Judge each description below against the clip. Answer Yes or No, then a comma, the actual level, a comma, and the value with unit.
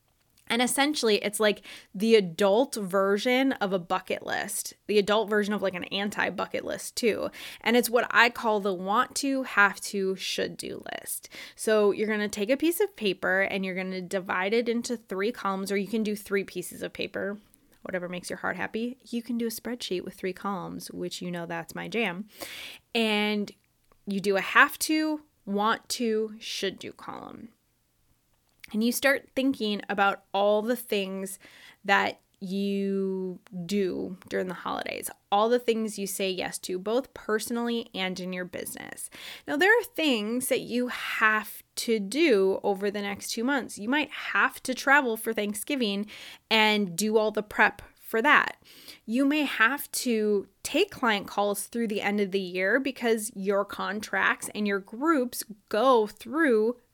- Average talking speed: Yes, average, 175 wpm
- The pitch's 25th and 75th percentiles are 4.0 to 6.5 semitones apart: No, average, 3.3 semitones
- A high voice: Yes, high, 215 Hz